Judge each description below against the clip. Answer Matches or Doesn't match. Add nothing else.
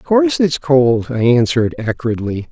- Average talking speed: Matches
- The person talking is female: Doesn't match